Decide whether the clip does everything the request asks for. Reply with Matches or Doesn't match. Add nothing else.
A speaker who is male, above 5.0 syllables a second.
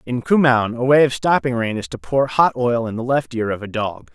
Matches